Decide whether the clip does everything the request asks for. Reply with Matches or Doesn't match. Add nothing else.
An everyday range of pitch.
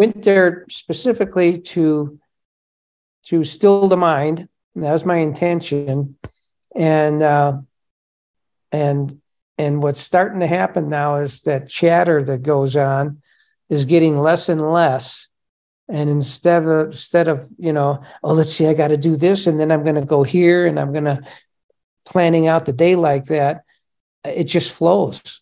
Matches